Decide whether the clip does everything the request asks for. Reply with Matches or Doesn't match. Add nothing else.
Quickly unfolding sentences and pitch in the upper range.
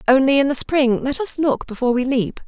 Matches